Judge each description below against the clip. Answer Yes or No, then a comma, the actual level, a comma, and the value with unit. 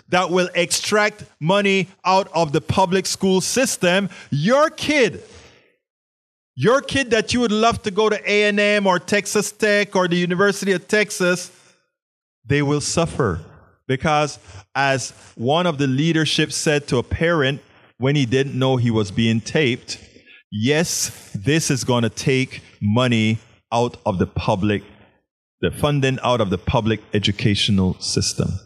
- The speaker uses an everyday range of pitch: No, wide, 8.5 semitones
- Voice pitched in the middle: Yes, medium, 150 Hz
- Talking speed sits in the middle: Yes, average, 145 wpm